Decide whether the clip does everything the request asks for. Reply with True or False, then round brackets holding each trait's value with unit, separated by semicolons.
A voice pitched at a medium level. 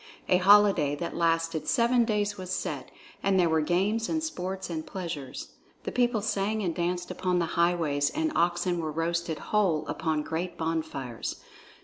True (175 Hz)